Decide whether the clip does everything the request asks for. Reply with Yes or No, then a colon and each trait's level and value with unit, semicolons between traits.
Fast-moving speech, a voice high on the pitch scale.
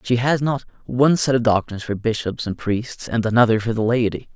No: fast, 220 wpm; low, 115 Hz